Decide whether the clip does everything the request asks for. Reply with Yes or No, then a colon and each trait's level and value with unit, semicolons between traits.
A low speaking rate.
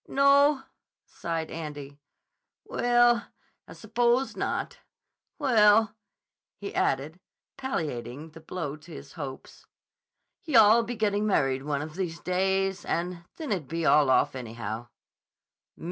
Yes: slow, 115 wpm